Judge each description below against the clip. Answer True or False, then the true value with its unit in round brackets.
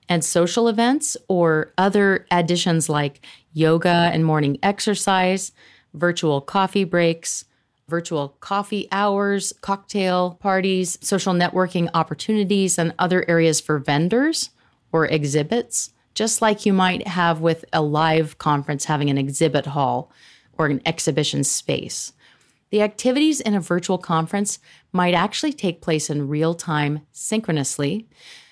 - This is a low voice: False (175 Hz)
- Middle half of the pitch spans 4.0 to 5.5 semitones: True (4.3 semitones)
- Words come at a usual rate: False (125 wpm)